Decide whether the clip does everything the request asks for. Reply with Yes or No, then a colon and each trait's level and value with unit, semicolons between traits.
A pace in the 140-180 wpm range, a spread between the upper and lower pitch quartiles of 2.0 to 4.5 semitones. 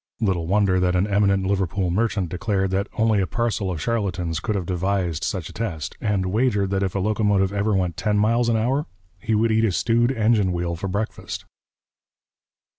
No: average, 190 wpm; average, 2.9 semitones